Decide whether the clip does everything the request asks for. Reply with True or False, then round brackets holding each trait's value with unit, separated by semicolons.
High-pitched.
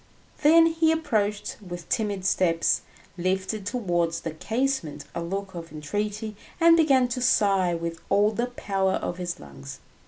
True (200 Hz)